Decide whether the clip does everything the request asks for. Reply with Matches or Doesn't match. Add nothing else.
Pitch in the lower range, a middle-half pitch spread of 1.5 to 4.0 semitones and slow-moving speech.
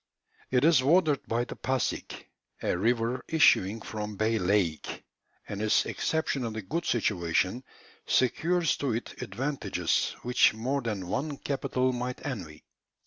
Doesn't match